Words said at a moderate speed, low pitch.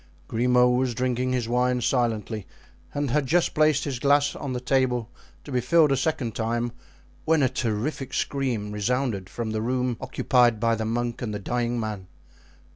Yes: average, 175 wpm; low, 125 Hz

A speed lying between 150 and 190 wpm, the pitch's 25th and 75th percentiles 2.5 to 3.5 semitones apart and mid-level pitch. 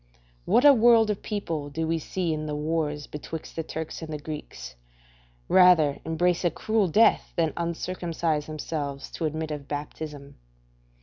Yes: average, 160 wpm; average, 2.8 semitones; medium, 160 Hz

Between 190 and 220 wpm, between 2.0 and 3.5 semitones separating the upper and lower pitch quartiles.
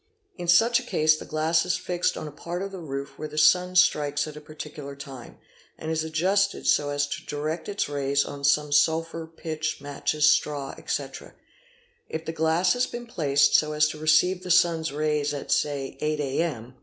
Yes: average, 195 wpm; average, 2.8 semitones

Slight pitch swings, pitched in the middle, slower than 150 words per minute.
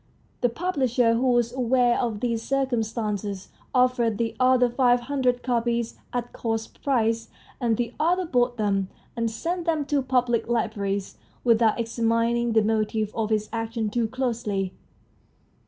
No: narrow, 2.1 semitones; high, 235 Hz; average, 140 wpm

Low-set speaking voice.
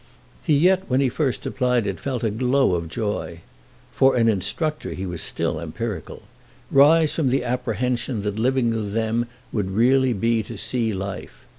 Yes: low, 115 Hz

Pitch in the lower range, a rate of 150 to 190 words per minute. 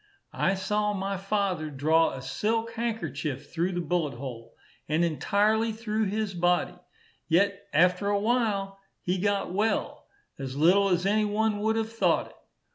No: high, 195 Hz; average, 155 wpm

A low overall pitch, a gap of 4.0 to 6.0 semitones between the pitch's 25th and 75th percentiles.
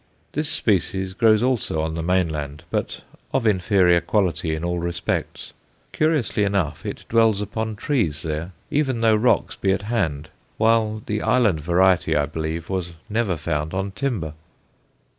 Yes: very low, 95 Hz; average, 5.2 semitones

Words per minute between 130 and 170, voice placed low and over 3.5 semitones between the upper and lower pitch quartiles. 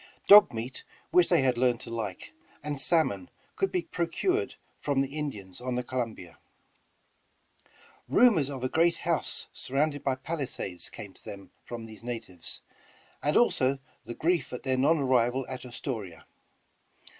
Yes: average, 150 wpm; low, 130 Hz; average, 4.8 semitones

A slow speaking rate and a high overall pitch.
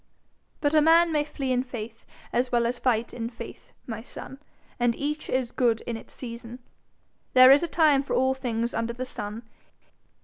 No: average, 190 wpm; very high, 250 Hz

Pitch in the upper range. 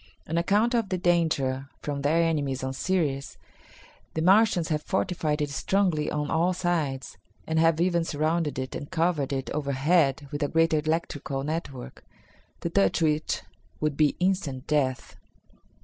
No: medium, 155 Hz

